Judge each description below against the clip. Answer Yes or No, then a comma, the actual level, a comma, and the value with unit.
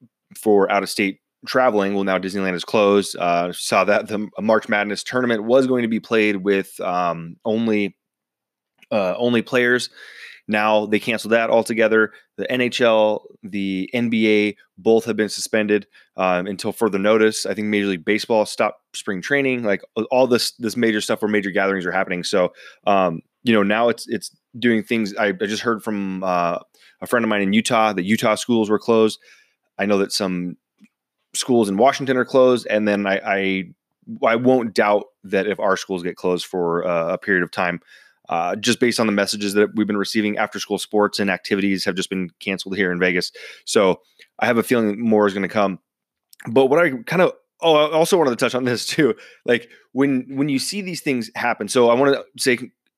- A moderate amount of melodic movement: Yes, average, 3.2 semitones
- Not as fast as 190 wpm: No, average, 200 wpm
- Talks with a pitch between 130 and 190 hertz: No, low, 105 Hz